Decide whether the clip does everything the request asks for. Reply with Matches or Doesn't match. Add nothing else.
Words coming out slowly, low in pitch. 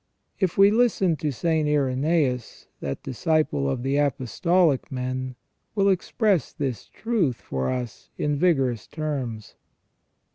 Doesn't match